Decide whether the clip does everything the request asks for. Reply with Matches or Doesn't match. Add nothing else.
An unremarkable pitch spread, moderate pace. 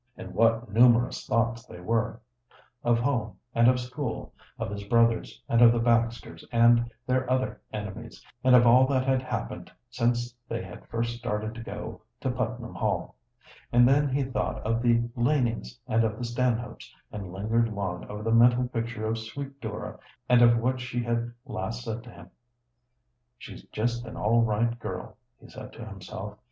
Doesn't match